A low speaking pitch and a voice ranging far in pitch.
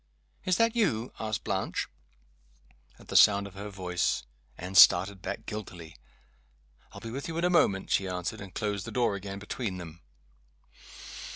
No: low, 100 Hz; average, 3.7 semitones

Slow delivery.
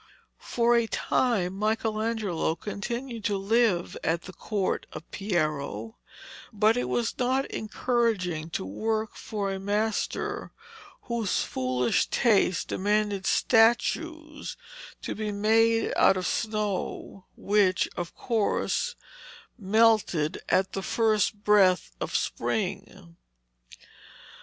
Yes: slow, 105 wpm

